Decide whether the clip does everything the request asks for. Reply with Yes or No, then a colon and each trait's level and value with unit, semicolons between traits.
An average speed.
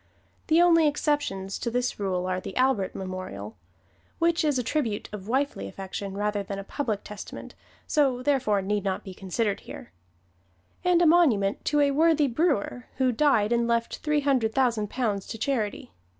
Yes: average, 170 wpm